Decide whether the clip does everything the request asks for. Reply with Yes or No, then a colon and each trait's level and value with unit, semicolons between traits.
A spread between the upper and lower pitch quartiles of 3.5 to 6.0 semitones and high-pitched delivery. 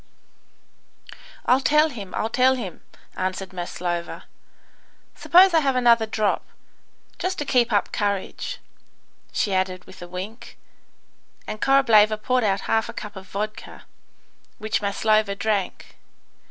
Yes: average, 4.5 semitones; high, 215 Hz